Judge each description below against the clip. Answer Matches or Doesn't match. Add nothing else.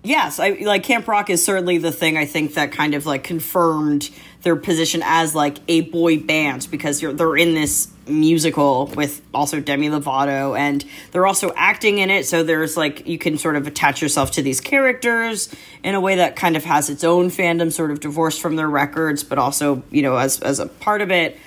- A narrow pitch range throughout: Doesn't match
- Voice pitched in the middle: Matches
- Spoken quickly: Matches